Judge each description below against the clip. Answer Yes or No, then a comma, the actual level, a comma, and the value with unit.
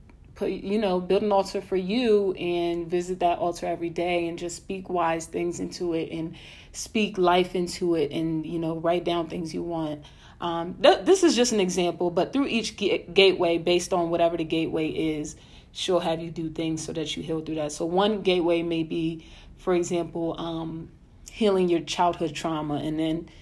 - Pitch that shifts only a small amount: Yes, narrow, 1.9 semitones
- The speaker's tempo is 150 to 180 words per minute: No, average, 195 wpm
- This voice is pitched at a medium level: Yes, medium, 170 Hz